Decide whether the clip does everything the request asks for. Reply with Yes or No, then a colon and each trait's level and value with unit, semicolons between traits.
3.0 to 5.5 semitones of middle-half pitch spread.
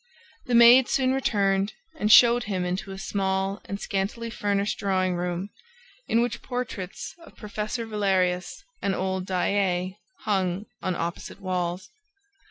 No: narrow, 2.5 semitones